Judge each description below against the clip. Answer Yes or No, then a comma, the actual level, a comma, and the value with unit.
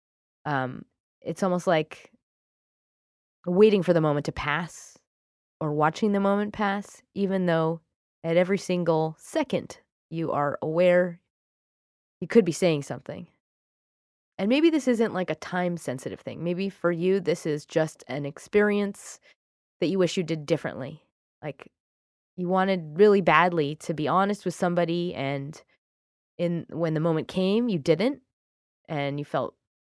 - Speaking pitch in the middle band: Yes, medium, 170 Hz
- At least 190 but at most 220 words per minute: No, average, 145 wpm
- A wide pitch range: No, average, 4.0 semitones